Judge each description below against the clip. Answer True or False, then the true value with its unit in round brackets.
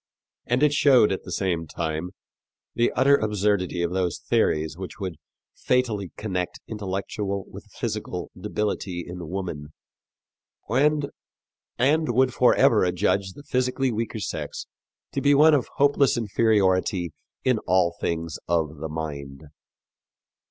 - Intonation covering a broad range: True (6.3 semitones)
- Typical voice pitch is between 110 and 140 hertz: False (100 Hz)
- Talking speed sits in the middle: False (125 wpm)